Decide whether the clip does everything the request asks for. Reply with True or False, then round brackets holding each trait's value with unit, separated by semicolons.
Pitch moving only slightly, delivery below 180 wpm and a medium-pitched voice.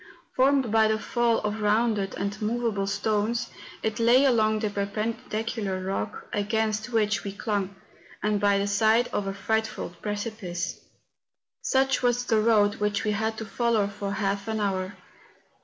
False (2.0 semitones; 155 wpm; 215 Hz)